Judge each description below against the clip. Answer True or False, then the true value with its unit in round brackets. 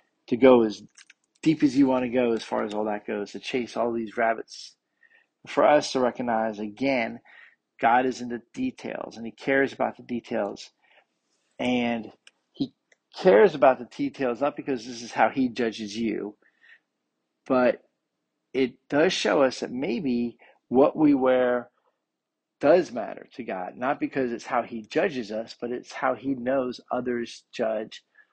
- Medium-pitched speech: False (125 Hz)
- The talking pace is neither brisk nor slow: True (165 wpm)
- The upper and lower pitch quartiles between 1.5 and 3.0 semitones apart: True (2.6 semitones)